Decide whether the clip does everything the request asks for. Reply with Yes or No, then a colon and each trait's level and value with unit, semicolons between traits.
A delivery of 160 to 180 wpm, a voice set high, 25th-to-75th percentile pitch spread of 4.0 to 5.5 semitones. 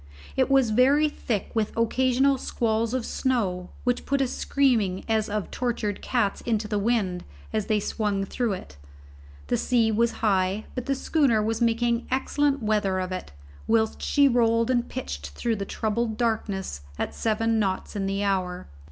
No: average, 170 wpm; high, 225 Hz; average, 3.3 semitones